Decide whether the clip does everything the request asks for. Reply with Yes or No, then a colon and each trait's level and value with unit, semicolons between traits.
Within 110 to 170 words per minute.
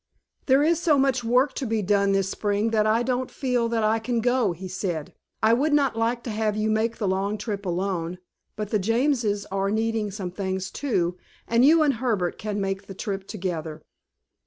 No: average, 200 wpm